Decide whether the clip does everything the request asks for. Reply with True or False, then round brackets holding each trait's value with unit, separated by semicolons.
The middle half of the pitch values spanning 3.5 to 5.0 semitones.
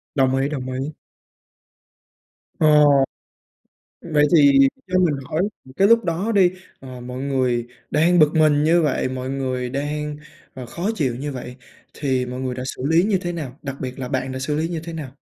True (3.9 semitones)